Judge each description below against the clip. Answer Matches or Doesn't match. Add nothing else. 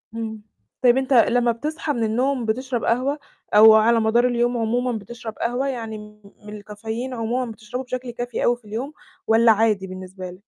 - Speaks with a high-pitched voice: Matches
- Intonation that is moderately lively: Doesn't match